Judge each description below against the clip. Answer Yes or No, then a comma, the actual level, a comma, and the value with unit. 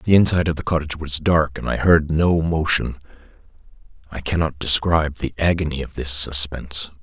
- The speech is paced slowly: No, average, 170 wpm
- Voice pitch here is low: Yes, very low, 75 Hz